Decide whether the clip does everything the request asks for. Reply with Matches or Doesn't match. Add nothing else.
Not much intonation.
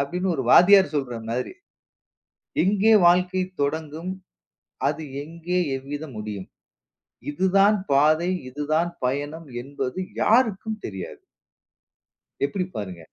Doesn't match